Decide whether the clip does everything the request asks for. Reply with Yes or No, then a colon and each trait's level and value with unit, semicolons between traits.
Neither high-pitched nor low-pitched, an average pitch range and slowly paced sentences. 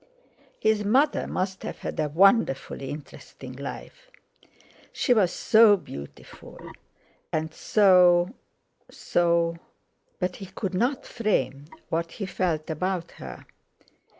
Yes: medium, 180 Hz; average, 4.8 semitones; slow, 100 wpm